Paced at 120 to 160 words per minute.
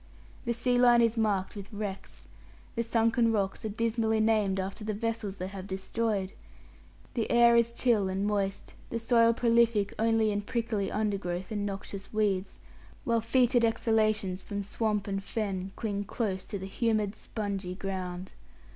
Yes: average, 155 wpm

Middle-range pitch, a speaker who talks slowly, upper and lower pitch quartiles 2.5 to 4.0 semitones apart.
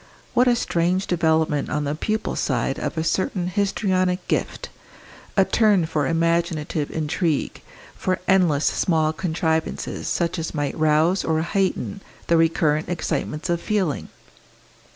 Yes: medium, 165 Hz; slow, 130 wpm; average, 2.8 semitones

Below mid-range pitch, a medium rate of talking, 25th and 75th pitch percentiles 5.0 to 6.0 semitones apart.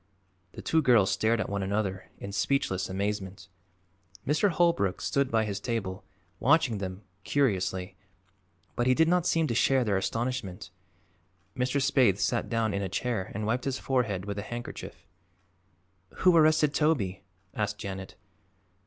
Yes: low, 110 Hz; average, 150 wpm; wide, 5.5 semitones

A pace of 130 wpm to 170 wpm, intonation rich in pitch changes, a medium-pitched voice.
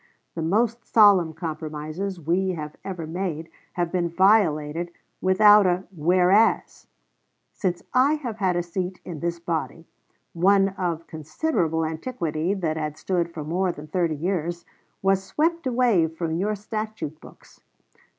No: average, 140 wpm; average, 3.4 semitones; medium, 175 Hz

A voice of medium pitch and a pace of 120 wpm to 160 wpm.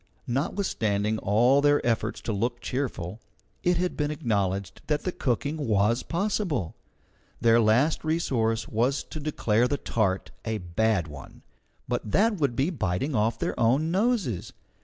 No: low, 120 Hz; average, 150 wpm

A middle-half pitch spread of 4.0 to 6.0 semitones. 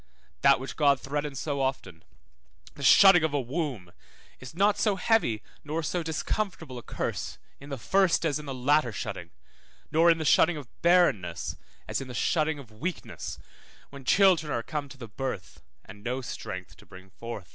Yes: average, 4.9 semitones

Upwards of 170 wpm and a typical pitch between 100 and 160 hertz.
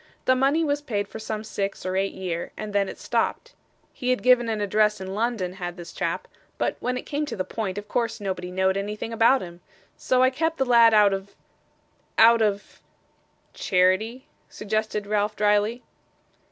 No: average, 190 wpm; high, 210 Hz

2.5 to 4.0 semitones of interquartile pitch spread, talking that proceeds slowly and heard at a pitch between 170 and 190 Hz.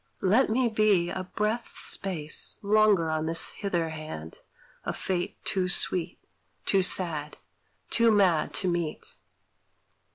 No: average, 4.4 semitones; slow, 125 wpm; medium, 185 Hz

